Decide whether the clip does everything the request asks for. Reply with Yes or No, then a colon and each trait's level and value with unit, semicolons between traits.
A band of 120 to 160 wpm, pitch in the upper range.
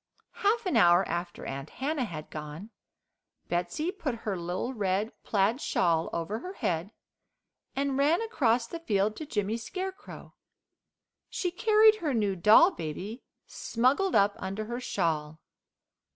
Yes: slow, 135 wpm; high, 220 Hz